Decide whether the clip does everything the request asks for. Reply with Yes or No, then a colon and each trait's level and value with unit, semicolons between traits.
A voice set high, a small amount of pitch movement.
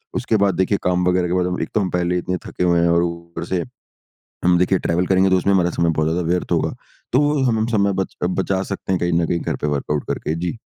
No: very low, 90 Hz; narrow, 1.8 semitones